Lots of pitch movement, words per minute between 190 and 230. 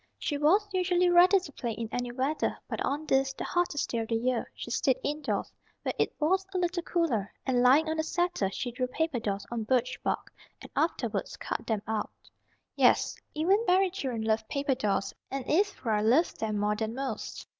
Yes: wide, 6.7 semitones; average, 200 wpm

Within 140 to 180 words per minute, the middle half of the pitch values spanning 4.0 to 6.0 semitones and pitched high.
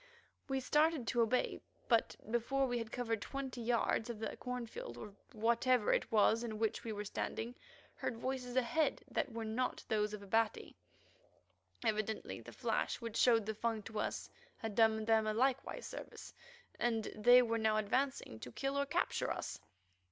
No: average, 170 wpm; narrow, 2.4 semitones; high, 230 Hz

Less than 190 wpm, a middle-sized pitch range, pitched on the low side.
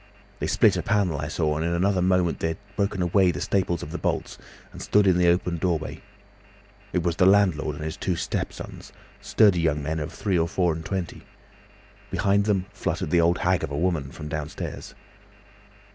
No: fast, 205 wpm; average, 3.0 semitones; very low, 85 Hz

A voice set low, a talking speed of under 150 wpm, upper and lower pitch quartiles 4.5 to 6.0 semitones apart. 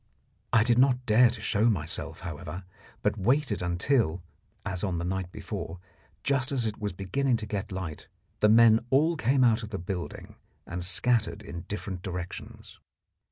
No: low, 105 Hz; average, 165 wpm; average, 4.9 semitones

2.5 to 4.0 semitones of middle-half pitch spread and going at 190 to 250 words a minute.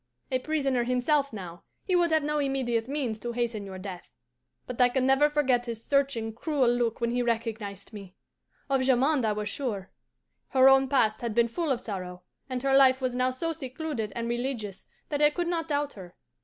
Yes: average, 3.7 semitones; average, 200 wpm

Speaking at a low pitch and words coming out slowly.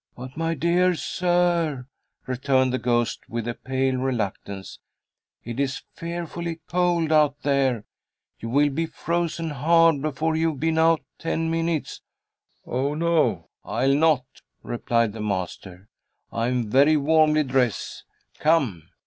No: medium, 145 Hz; slow, 130 wpm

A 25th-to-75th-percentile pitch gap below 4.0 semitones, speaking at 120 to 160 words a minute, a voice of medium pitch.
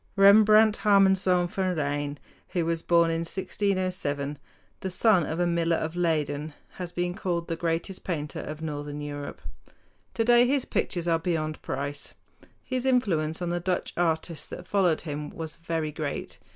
Yes: average, 3.3 semitones; average, 155 wpm; medium, 170 Hz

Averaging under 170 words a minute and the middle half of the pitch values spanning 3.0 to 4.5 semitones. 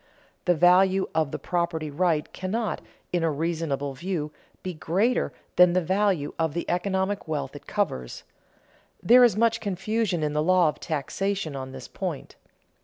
Yes: average, 160 wpm; average, 4.1 semitones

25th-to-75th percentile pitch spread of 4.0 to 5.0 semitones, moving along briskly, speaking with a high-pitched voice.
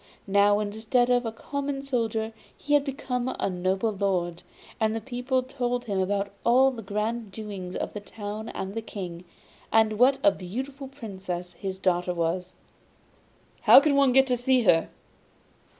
No: average, 4.7 semitones; average, 165 wpm; high, 220 Hz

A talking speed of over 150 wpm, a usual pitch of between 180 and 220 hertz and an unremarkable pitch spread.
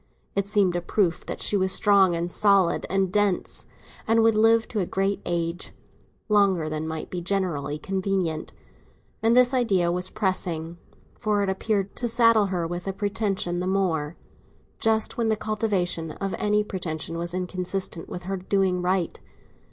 Yes: average, 160 wpm; high, 190 Hz; average, 3.0 semitones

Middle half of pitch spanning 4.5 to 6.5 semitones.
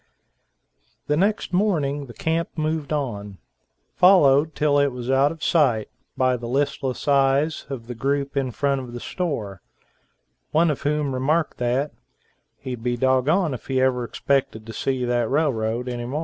No: average, 3.3 semitones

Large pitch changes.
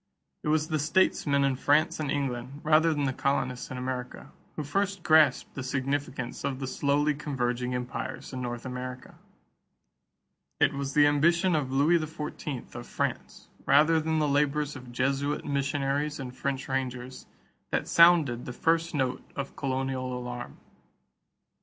No: average, 2.8 semitones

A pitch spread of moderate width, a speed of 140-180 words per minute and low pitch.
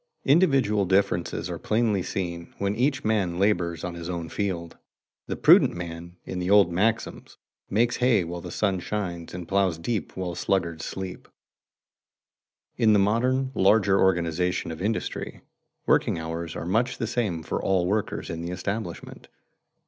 Yes: average, 3.9 semitones; average, 155 wpm; very low, 95 Hz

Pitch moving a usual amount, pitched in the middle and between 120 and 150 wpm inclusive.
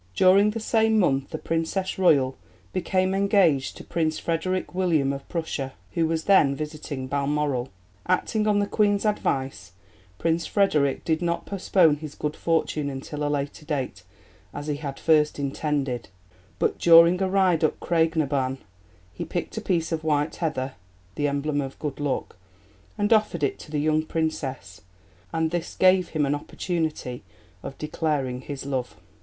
No: average, 4.0 semitones; medium, 155 Hz; average, 165 wpm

